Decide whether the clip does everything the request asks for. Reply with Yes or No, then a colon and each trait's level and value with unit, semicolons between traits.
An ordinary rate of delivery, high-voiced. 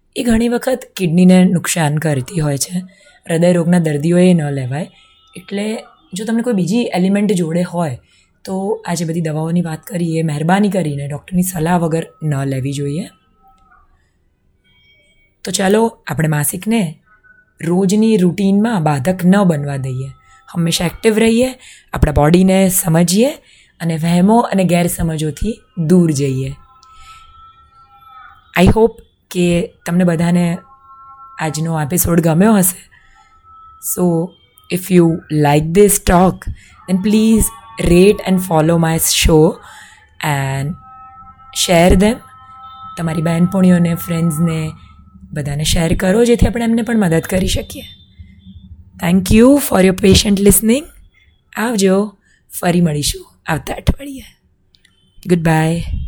No: average, 115 wpm; medium, 180 Hz